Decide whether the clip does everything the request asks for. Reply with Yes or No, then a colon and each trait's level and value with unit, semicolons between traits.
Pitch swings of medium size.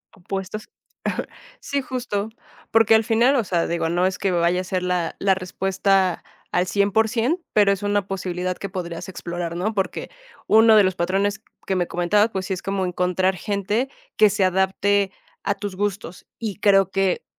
No: narrow, 2.2 semitones